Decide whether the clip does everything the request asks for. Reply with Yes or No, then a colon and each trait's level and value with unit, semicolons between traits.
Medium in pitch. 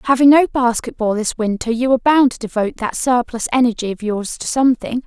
No: high, 240 Hz